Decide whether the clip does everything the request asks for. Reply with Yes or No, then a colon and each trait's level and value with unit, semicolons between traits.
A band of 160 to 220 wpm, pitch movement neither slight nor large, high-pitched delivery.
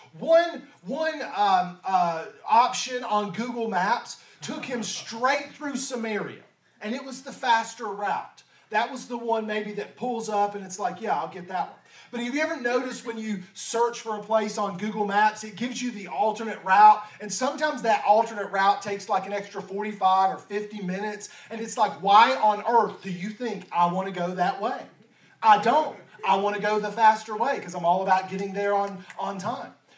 Yes: average, 200 wpm; average, 3.1 semitones; high, 215 Hz